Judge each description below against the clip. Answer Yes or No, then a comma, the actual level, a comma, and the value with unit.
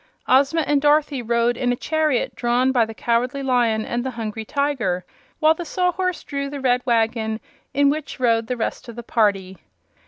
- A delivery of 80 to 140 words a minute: No, average, 185 wpm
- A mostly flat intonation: No, average, 3.7 semitones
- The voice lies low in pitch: No, very high, 250 Hz